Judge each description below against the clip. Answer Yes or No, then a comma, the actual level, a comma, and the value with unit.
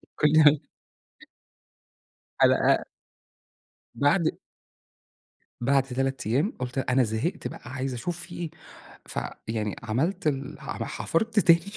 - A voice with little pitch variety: No, average, 4.7 semitones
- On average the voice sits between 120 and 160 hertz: Yes, low, 135 Hz